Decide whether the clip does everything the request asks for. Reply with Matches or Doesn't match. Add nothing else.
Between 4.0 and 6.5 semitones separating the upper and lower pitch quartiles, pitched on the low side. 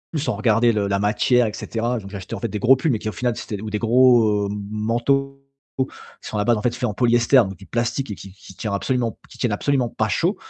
Doesn't match